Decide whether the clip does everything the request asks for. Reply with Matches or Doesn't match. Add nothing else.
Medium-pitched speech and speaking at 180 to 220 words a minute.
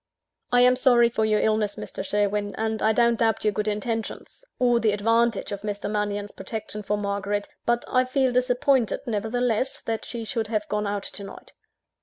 Doesn't match